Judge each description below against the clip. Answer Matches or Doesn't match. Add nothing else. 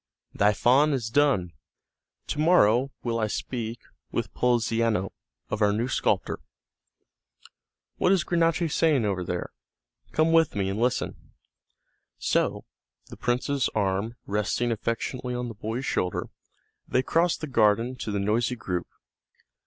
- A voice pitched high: Doesn't match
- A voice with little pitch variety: Doesn't match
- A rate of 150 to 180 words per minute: Doesn't match